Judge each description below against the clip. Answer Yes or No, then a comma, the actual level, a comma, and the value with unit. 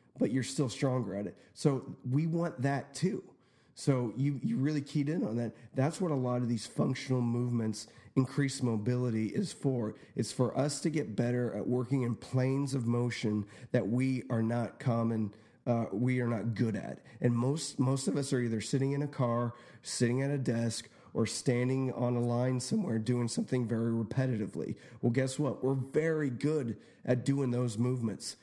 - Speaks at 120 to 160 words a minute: No, average, 195 wpm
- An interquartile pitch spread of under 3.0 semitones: Yes, narrow, 2.6 semitones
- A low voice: Yes, low, 125 Hz